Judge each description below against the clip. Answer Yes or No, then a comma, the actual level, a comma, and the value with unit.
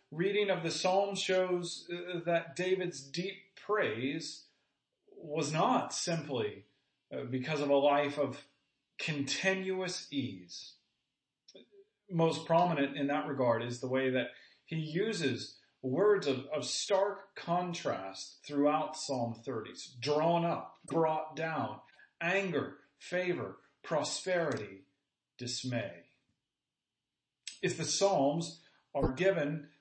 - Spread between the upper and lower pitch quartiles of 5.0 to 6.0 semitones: No, average, 4.6 semitones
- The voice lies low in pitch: No, medium, 155 Hz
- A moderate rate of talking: No, slow, 105 wpm